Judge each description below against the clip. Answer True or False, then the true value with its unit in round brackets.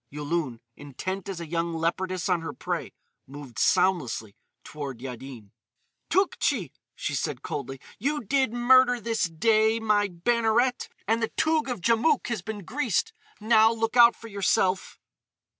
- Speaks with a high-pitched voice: True (200 Hz)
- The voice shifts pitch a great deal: True (6.3 semitones)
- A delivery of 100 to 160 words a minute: True (140 wpm)